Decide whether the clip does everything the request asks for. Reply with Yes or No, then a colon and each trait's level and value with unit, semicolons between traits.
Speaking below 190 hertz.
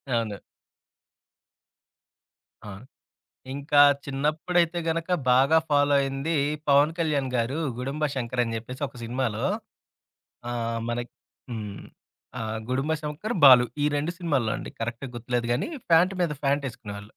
Yes: low, 135 Hz